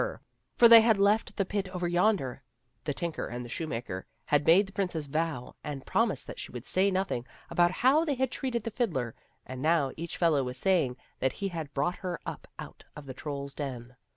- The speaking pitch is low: No, medium, 165 Hz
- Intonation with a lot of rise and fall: Yes, wide, 6.4 semitones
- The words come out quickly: Yes, fast, 210 wpm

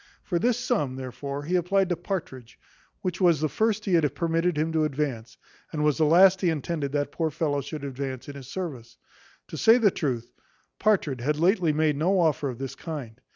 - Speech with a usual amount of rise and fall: Yes, average, 4.4 semitones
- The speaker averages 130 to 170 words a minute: No, average, 200 wpm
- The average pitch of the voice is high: No, medium, 155 Hz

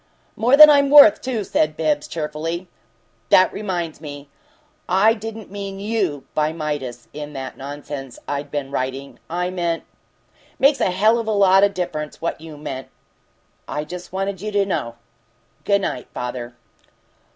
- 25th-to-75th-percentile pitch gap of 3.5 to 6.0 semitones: Yes, wide, 5.5 semitones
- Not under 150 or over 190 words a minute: Yes, average, 160 wpm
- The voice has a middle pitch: Yes, medium, 170 Hz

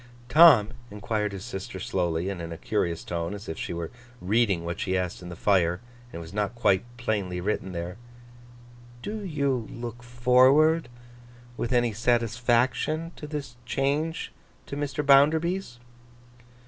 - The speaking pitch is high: No, low, 115 Hz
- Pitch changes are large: Yes, wide, 6.7 semitones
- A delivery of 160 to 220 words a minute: No, average, 150 wpm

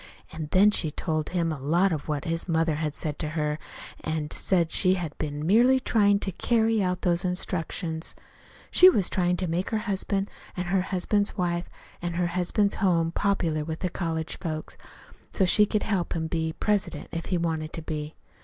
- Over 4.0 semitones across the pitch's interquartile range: No, average, 3.3 semitones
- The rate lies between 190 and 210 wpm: Yes, average, 200 wpm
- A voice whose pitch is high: No, medium, 175 Hz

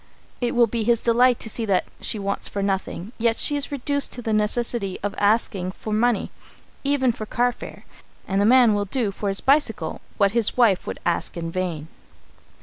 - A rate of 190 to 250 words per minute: Yes, average, 195 wpm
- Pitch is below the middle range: No, high, 220 Hz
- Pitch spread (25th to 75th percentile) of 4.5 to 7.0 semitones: No, average, 3.4 semitones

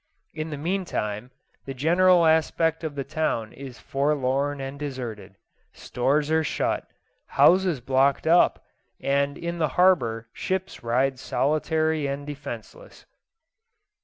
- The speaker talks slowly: Yes, slow, 120 wpm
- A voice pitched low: No, medium, 145 Hz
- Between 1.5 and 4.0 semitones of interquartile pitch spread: Yes, average, 3.3 semitones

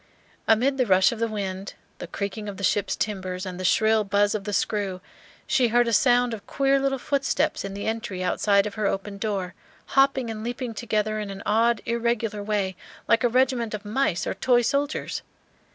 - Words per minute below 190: No, average, 200 wpm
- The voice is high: Yes, high, 215 Hz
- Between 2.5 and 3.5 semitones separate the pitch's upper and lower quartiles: Yes, average, 3.2 semitones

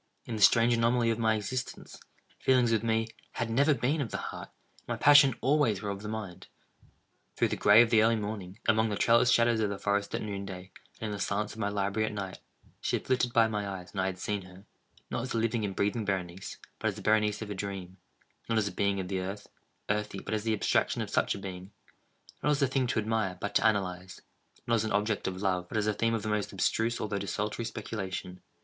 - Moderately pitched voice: No, low, 105 Hz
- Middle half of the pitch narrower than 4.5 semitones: Yes, narrow, 2.6 semitones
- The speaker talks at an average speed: No, fast, 235 wpm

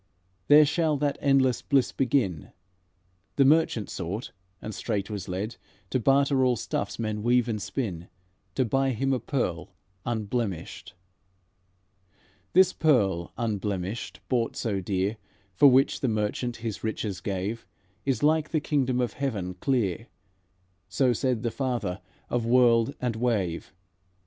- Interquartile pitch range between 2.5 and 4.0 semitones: No, average, 4.5 semitones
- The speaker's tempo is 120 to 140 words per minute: Yes, slow, 135 wpm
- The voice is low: Yes, low, 120 Hz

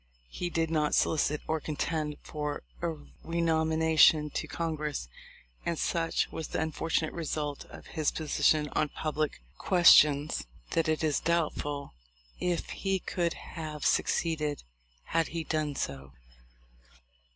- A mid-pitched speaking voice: Yes, medium, 155 Hz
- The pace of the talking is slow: Yes, slow, 130 wpm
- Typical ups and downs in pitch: No, narrow, 1.7 semitones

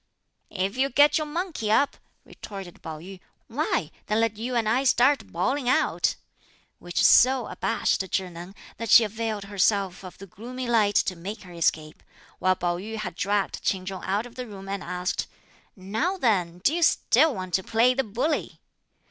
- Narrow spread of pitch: No, average, 5.2 semitones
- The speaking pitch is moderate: No, high, 210 Hz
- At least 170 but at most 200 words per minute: Yes, average, 180 wpm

